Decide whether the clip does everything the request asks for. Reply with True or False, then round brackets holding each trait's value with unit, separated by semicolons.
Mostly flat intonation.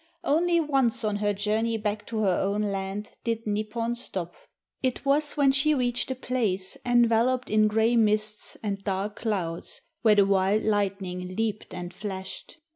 False (3.3 semitones)